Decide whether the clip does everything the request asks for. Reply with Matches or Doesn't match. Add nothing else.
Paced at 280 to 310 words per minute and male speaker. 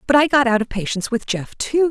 Doesn't match